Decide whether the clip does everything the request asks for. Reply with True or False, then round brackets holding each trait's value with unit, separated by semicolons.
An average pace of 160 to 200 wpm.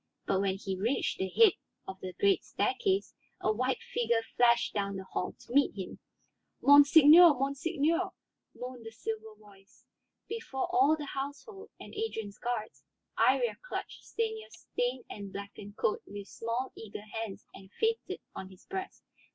False (150 wpm)